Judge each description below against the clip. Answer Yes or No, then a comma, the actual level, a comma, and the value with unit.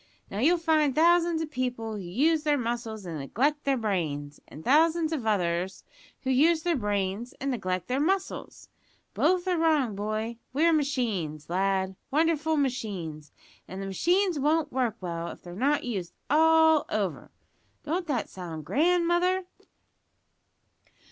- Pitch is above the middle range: Yes, very high, 255 Hz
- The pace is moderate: Yes, average, 150 wpm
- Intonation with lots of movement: Yes, wide, 8.6 semitones